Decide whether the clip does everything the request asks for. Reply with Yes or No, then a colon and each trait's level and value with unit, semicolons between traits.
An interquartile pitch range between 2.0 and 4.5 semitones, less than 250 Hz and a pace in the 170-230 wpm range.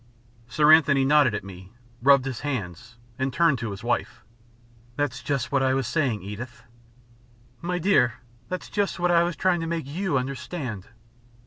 No: wide, 5.4 semitones; low, 135 Hz; average, 175 wpm